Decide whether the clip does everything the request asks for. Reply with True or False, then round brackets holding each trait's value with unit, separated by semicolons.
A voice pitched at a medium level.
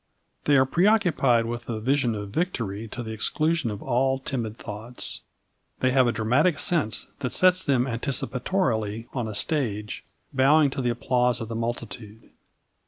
False (125 Hz)